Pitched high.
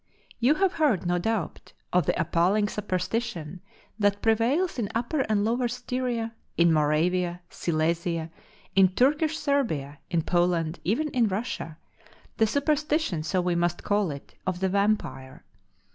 Yes: high, 200 Hz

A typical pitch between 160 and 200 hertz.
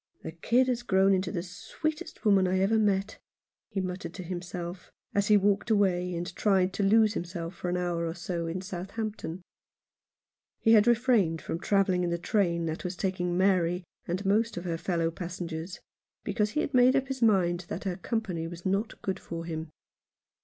Yes: medium, 185 Hz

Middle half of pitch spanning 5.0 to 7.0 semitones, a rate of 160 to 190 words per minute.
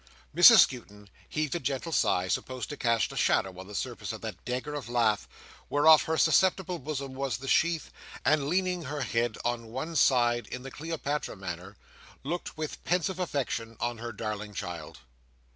Yes: wide, 5.5 semitones; average, 175 wpm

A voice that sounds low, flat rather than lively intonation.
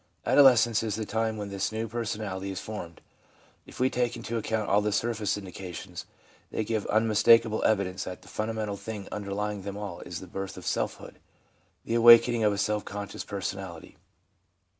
Yes: low, 105 Hz; narrow, 2.3 semitones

